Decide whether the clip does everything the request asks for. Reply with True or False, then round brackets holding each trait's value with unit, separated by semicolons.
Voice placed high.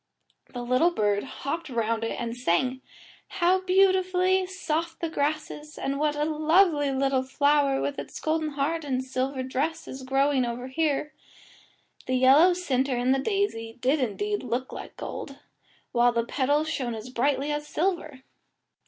True (280 Hz)